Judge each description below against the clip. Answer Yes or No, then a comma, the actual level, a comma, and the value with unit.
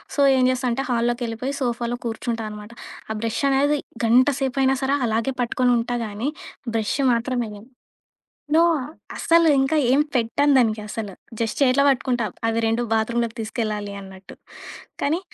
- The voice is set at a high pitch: Yes, high, 240 Hz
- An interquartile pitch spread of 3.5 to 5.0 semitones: No, average, 3.0 semitones